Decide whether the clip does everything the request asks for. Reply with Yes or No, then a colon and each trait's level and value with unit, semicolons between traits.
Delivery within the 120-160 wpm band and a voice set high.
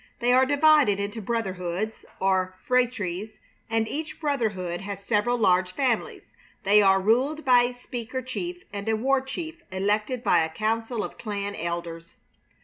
Yes: average, 150 wpm; high, 220 Hz